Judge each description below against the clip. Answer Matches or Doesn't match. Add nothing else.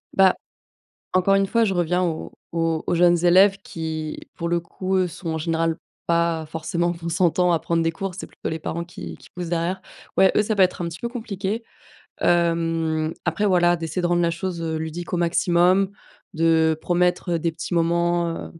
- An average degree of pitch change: Doesn't match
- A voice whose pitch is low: Doesn't match